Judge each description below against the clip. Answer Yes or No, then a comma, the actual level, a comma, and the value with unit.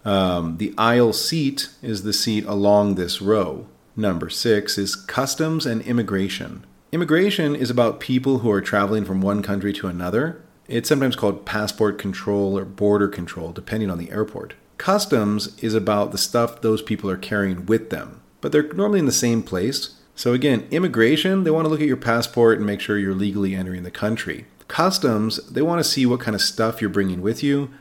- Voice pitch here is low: Yes, low, 110 Hz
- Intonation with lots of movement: No, average, 4.1 semitones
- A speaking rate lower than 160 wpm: No, average, 190 wpm